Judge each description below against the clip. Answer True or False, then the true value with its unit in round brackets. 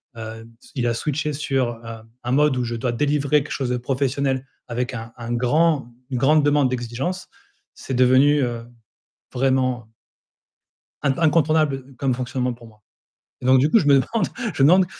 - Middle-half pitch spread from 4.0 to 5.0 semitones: False (3.2 semitones)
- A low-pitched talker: True (130 Hz)